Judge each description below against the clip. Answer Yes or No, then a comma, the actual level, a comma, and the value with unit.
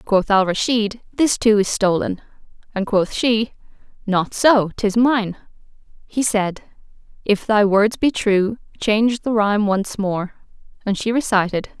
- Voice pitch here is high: Yes, high, 210 Hz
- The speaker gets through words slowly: No, average, 145 wpm